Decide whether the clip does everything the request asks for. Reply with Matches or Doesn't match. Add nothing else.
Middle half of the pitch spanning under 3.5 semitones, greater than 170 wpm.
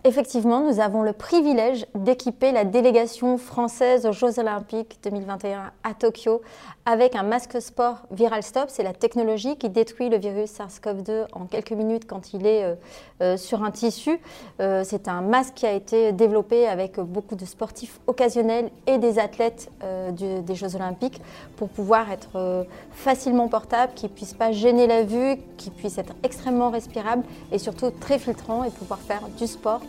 Doesn't match